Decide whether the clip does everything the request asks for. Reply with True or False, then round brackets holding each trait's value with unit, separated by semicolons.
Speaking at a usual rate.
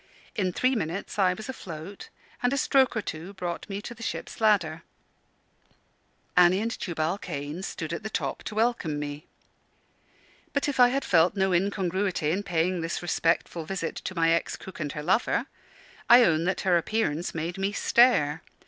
True (175 wpm)